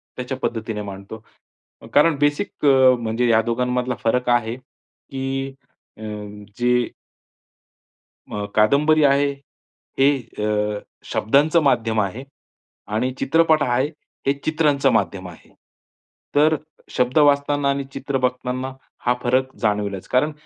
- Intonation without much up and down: No, average, 3.9 semitones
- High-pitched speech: No, low, 125 Hz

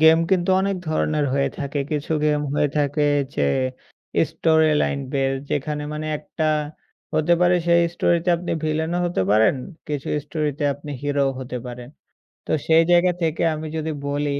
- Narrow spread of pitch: Yes, narrow, 2.1 semitones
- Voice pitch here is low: No, medium, 150 Hz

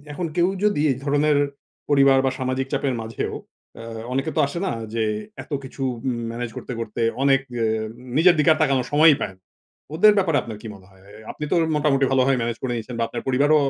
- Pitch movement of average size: Yes, average, 3.7 semitones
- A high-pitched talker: No, low, 135 Hz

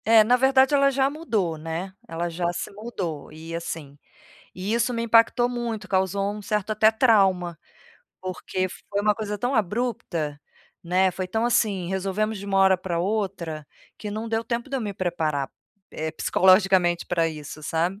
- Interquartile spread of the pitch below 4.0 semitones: No, average, 4.4 semitones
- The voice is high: Yes, high, 195 Hz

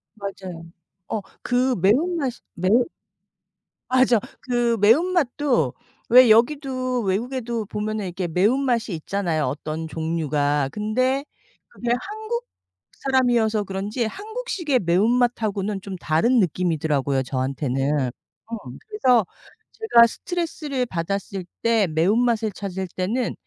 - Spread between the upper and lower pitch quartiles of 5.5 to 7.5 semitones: Yes, wide, 6.0 semitones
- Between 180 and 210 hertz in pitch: No, high, 220 Hz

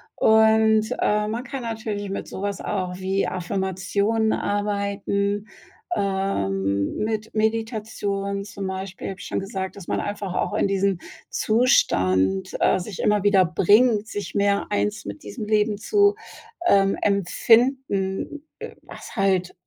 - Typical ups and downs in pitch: No, narrow, 2.3 semitones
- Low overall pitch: No, high, 200 Hz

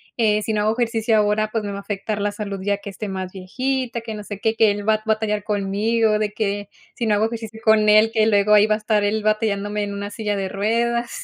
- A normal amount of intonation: No, narrow, 1.4 semitones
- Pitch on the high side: Yes, high, 210 Hz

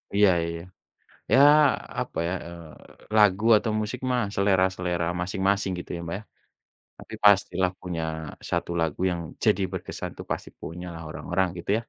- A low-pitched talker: Yes, very low, 95 Hz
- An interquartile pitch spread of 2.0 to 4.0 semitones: Yes, average, 2.7 semitones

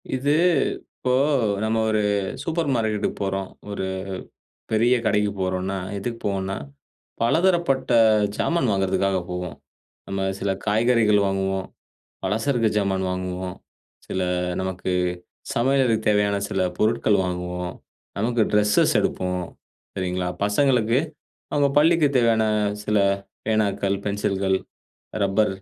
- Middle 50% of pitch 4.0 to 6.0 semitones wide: No, average, 3.4 semitones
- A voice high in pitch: No, low, 105 Hz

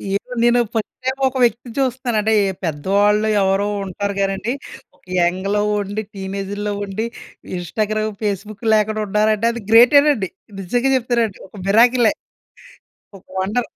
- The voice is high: Yes, high, 215 Hz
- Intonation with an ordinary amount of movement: Yes, average, 3.3 semitones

